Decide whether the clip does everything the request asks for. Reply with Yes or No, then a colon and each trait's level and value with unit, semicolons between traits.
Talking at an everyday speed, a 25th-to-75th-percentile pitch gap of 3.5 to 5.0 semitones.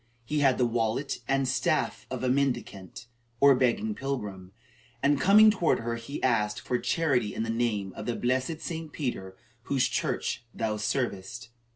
Yes: average, 165 wpm; average, 3.9 semitones